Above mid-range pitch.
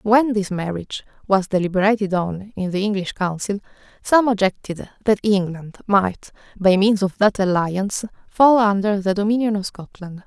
Yes: high, 200 Hz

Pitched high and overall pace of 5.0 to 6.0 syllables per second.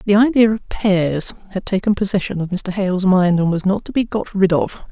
Yes: high, 195 Hz; 5.5 syllables/s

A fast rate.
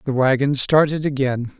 No: average, 150 wpm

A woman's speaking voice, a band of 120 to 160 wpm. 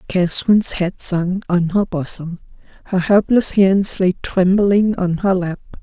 Yes: female; average, 145 wpm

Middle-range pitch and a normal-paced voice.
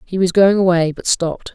No: medium, 180 Hz; fast, 235 wpm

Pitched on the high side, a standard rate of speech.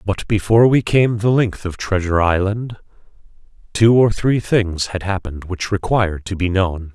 No: low, 100 Hz; average, 175 wpm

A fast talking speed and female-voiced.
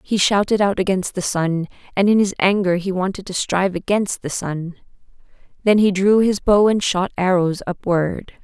No: average, 185 wpm; female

